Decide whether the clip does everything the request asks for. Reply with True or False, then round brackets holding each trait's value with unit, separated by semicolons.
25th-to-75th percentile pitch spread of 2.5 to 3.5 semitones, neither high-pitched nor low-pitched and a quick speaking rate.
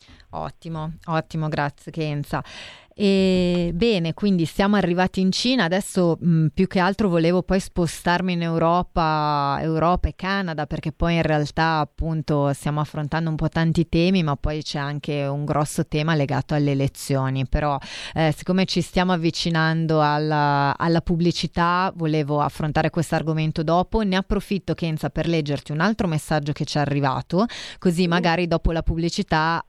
False (2.8 semitones; 160 Hz; 155 wpm)